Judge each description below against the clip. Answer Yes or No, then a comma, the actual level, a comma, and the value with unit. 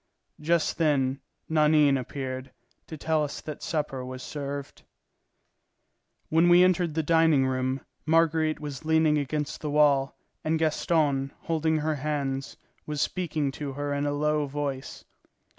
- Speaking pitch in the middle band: Yes, medium, 150 Hz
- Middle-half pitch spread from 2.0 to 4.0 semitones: Yes, narrow, 2.4 semitones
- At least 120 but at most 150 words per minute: Yes, average, 140 wpm